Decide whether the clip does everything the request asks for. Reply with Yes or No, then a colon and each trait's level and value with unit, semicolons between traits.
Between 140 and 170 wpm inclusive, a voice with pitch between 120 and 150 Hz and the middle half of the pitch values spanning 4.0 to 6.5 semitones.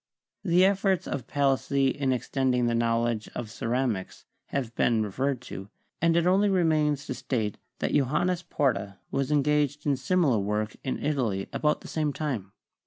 Yes: average, 160 wpm; low, 135 Hz; average, 4.5 semitones